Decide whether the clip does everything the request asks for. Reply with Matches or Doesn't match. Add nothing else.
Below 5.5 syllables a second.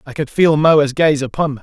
Matches